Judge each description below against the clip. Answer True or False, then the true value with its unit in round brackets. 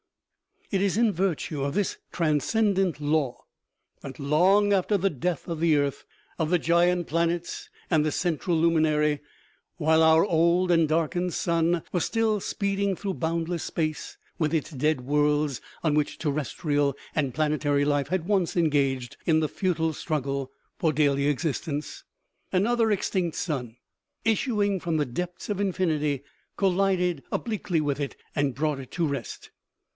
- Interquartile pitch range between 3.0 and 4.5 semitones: True (3.6 semitones)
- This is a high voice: False (160 Hz)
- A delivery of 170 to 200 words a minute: False (150 wpm)